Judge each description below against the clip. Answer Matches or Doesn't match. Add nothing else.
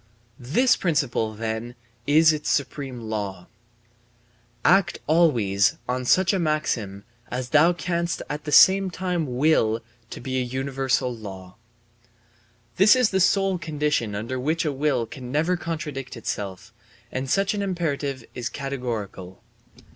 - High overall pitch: Doesn't match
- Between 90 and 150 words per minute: Matches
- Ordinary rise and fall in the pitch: Doesn't match